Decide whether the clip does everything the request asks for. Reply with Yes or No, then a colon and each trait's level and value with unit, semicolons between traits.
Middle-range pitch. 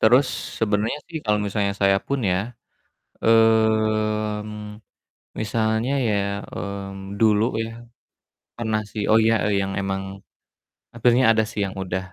No: low, 110 Hz